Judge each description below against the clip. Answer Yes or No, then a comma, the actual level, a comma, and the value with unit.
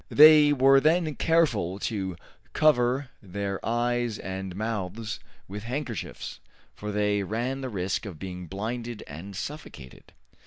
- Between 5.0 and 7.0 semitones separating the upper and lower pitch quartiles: Yes, wide, 5.4 semitones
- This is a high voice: No, low, 110 Hz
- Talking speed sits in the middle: No, slow, 125 wpm